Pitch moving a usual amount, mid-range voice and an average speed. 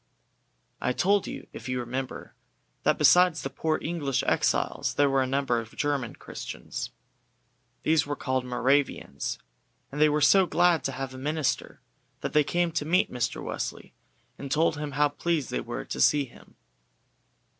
Yes: average, 3.4 semitones; medium, 145 Hz; average, 165 wpm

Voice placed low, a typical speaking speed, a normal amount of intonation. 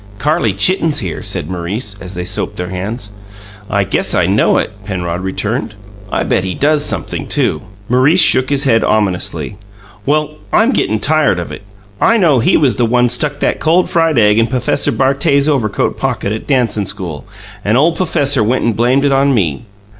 No: low, 120 Hz; average, 185 wpm; wide, 6.1 semitones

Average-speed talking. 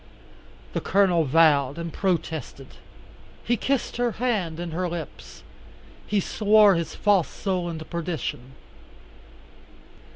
No: slow, 110 wpm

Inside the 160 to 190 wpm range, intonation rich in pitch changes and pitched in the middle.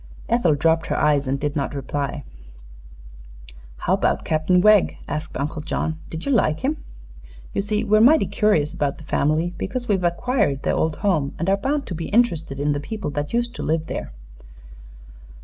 Yes: average, 185 wpm; wide, 6.4 semitones; medium, 165 Hz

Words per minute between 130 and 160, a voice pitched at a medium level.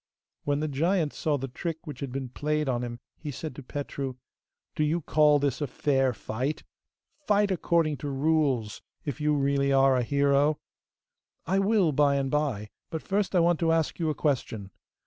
No: average, 185 wpm; medium, 145 Hz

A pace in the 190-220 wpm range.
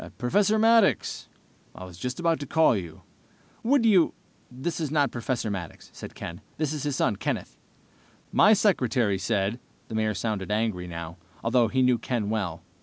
No: average, 165 wpm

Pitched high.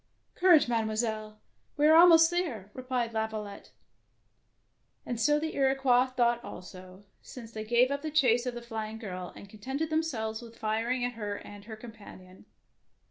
Yes: high, 235 Hz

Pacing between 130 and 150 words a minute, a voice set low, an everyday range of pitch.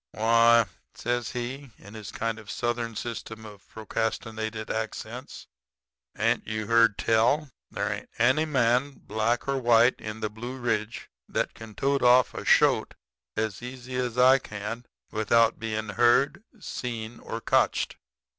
No: average, 145 wpm; low, 115 Hz; narrow, 2.0 semitones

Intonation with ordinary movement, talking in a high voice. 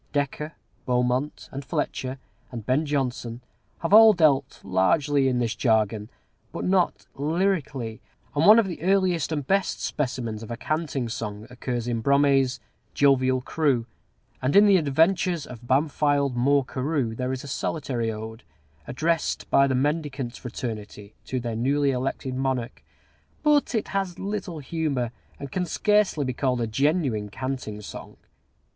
No: average, 4.4 semitones; low, 135 Hz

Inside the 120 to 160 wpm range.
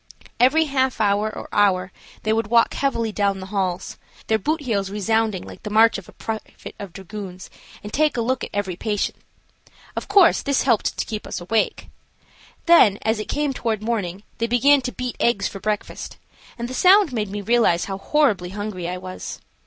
No: average, 190 wpm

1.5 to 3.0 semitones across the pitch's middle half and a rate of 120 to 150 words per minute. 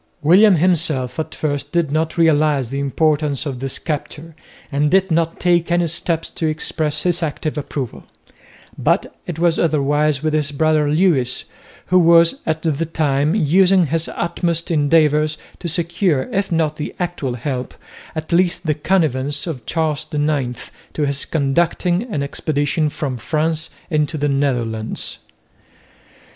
Yes: average, 2.7 semitones; average, 145 wpm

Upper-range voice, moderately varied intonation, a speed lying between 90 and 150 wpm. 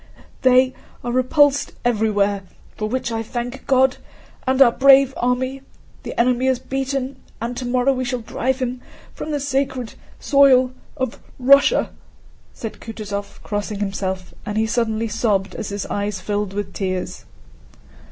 Yes: high, 245 Hz; average, 3.7 semitones; average, 140 wpm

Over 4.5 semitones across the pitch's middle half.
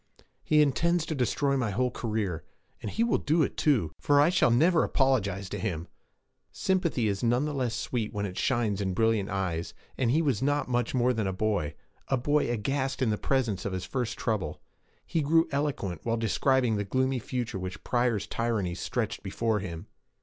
Yes: average, 5.1 semitones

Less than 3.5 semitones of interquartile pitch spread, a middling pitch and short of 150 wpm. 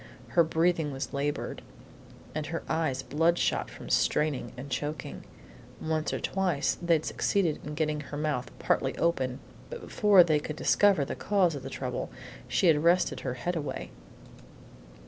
No: average, 2.8 semitones; medium, 155 Hz; average, 155 wpm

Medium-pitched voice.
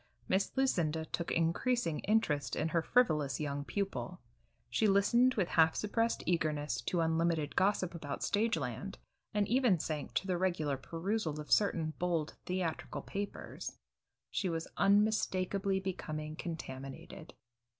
Yes: medium, 175 Hz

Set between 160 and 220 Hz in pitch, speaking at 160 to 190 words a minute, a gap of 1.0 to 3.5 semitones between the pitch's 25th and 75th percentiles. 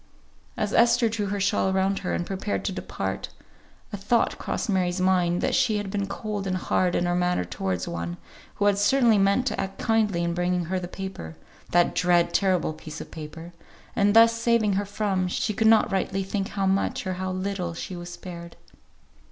No: high, 190 Hz; average, 200 wpm; narrow, 2.6 semitones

